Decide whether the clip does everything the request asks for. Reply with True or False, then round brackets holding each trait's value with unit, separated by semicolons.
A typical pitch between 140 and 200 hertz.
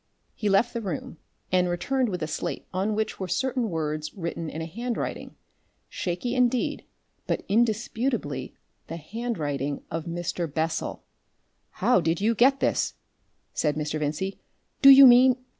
True (185 Hz)